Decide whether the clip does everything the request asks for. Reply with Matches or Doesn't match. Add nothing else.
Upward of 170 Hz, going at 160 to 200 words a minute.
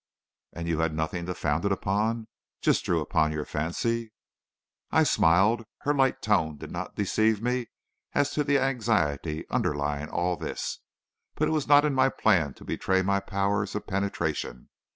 Doesn't match